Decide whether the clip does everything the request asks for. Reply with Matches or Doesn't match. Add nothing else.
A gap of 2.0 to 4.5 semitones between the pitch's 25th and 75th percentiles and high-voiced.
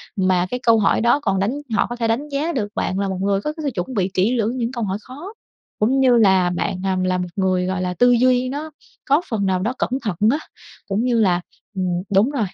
Doesn't match